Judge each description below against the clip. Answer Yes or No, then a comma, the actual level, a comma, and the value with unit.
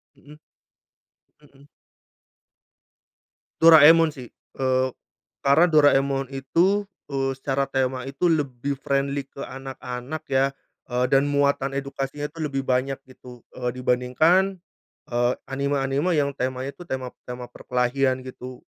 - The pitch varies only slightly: Yes, narrow, 2.0 semitones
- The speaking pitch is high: No, low, 135 Hz